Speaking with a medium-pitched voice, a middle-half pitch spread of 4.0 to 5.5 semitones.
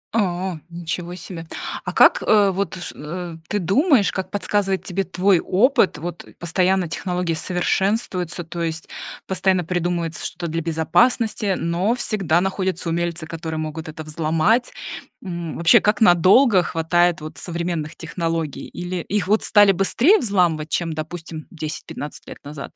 No: medium, 175 Hz; average, 2.8 semitones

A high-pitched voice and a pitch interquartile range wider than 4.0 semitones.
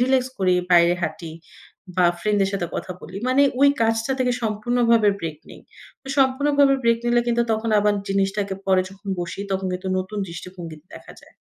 Yes: high, 205 Hz; average, 4.4 semitones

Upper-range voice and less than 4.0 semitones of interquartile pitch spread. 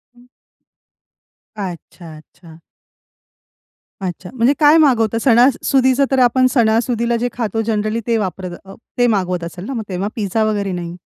No: high, 220 Hz; average, 4.6 semitones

